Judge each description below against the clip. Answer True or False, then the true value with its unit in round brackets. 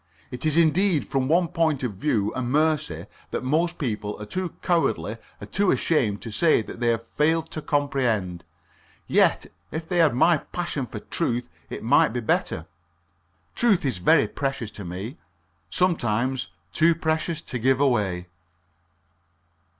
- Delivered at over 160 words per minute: False (155 wpm)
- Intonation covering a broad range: True (6.2 semitones)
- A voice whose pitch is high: False (135 Hz)